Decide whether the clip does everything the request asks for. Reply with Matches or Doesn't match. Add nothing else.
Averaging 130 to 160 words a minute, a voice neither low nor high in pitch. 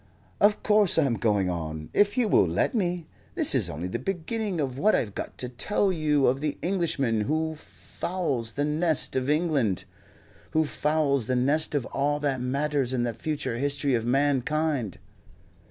Doesn't match